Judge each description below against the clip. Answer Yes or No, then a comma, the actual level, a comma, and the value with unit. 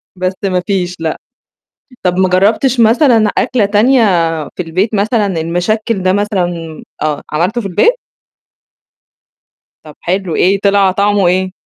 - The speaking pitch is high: Yes, high, 195 Hz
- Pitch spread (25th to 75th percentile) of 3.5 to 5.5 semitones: No, average, 3.0 semitones